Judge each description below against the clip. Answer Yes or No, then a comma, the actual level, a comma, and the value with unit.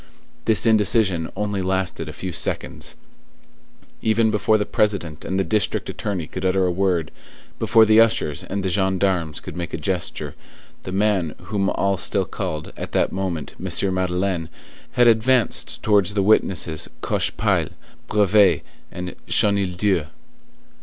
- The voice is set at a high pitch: No, very low, 95 Hz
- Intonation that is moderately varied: Yes, average, 3.0 semitones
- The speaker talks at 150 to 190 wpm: No, average, 140 wpm